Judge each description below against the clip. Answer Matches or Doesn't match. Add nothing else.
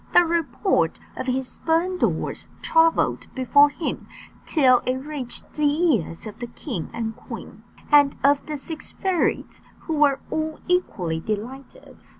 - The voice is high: Matches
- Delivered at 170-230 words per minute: Doesn't match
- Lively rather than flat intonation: Doesn't match